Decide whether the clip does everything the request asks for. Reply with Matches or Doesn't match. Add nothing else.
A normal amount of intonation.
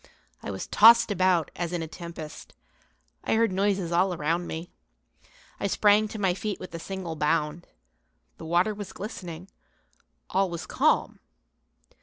Matches